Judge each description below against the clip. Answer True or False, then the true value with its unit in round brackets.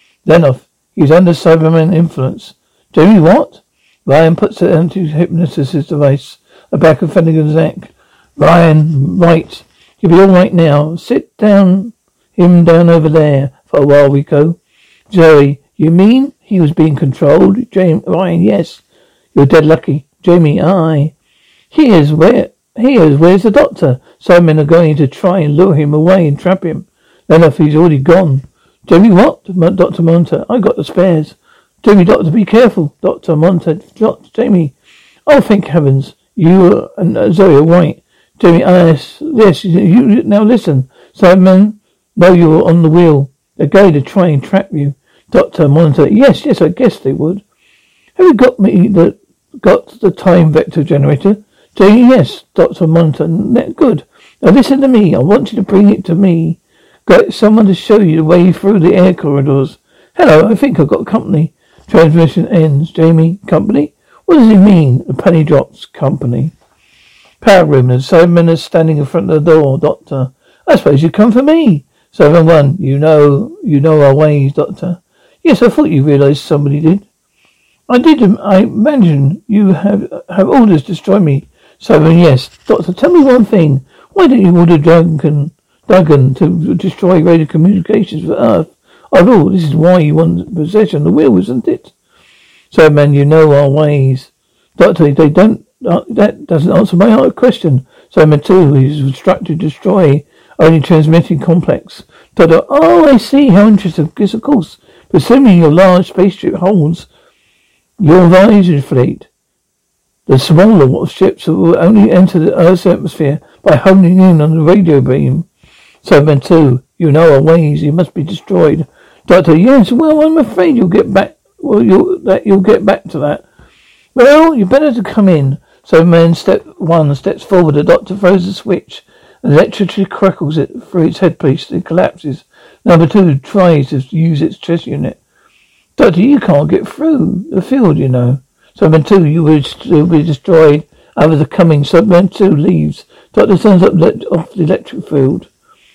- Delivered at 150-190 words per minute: True (170 wpm)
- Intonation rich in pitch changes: False (4.0 semitones)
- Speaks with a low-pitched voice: False (170 Hz)